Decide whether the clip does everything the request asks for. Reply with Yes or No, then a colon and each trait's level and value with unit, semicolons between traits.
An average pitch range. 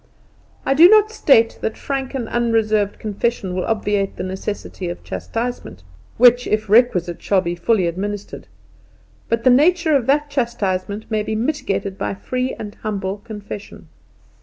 Yes: average, 4.0 semitones